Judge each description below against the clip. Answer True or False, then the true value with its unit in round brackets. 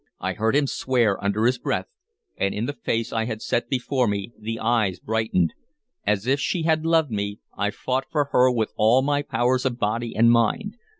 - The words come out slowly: False (200 wpm)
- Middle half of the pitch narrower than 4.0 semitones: True (3.5 semitones)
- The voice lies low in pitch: True (115 Hz)